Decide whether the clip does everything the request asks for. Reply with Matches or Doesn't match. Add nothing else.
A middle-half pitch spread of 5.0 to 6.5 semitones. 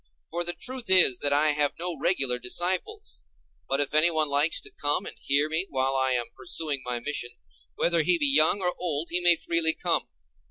Doesn't match